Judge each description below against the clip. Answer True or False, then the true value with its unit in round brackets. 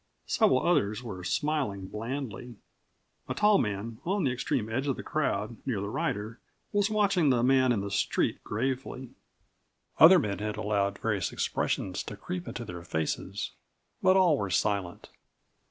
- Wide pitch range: True (5.9 semitones)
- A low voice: True (115 Hz)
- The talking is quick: False (155 wpm)